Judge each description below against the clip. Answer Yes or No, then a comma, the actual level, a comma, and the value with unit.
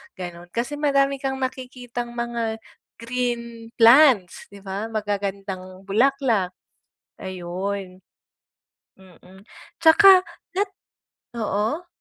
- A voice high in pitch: Yes, high, 225 Hz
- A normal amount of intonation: Yes, average, 5.0 semitones